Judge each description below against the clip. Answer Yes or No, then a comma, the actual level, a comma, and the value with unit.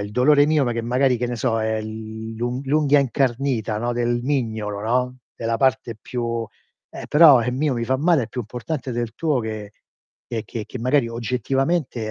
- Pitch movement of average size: Yes, average, 3.1 semitones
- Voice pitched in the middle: No, low, 120 Hz